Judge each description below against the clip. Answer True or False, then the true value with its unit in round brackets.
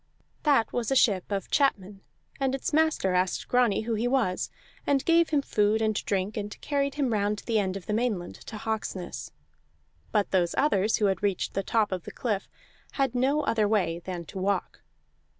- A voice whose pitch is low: False (215 Hz)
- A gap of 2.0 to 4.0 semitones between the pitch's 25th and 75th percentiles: False (4.7 semitones)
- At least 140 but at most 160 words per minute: False (190 wpm)